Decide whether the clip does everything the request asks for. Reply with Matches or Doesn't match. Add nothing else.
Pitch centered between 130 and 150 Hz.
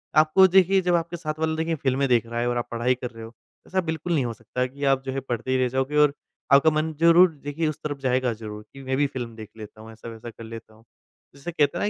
Matches